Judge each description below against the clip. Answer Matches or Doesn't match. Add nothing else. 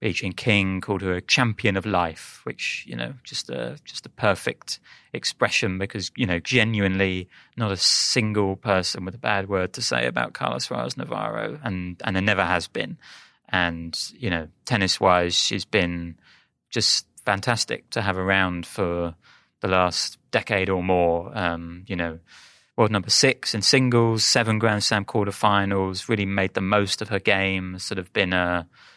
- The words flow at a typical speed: Matches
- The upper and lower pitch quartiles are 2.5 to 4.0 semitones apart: Matches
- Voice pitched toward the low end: Matches